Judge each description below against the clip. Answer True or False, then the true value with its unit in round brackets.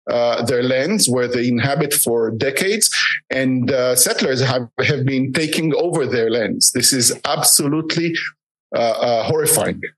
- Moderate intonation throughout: True (4.3 semitones)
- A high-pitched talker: False (130 Hz)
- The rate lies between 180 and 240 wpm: False (145 wpm)